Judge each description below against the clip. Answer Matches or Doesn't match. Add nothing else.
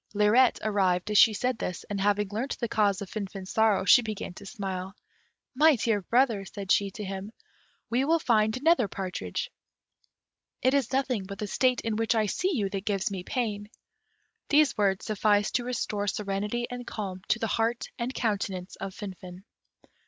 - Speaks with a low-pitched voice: Doesn't match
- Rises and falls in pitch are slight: Doesn't match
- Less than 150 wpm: Doesn't match